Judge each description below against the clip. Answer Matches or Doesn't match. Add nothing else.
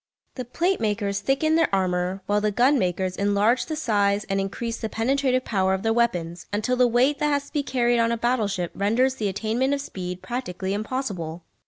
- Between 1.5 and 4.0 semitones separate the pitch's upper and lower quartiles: Doesn't match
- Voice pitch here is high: Matches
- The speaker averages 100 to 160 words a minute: Doesn't match